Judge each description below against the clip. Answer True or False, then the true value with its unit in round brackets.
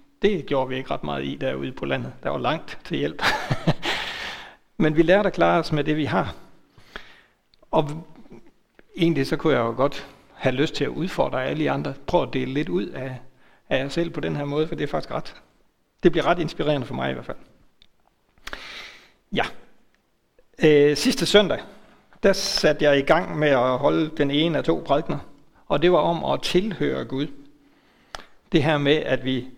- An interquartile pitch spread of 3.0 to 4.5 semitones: True (3.4 semitones)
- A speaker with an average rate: True (195 wpm)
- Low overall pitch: False (150 Hz)